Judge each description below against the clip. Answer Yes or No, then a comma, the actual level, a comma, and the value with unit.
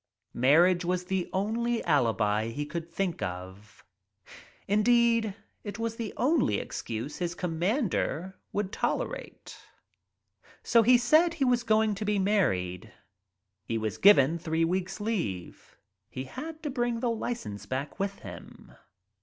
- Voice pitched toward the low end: No, high, 190 Hz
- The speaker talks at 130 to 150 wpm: Yes, slow, 135 wpm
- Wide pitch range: Yes, wide, 8.5 semitones